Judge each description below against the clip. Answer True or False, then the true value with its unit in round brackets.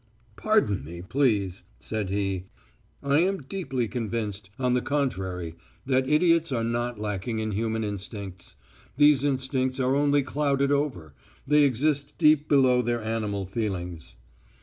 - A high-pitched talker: False (120 Hz)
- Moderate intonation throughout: False (5.7 semitones)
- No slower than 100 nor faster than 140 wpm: True (135 wpm)